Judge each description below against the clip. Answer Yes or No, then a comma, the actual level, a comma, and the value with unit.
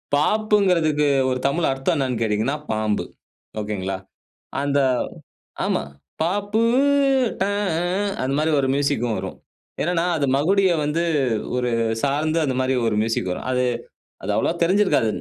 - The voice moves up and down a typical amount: No, wide, 6.1 semitones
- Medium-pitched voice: Yes, medium, 145 Hz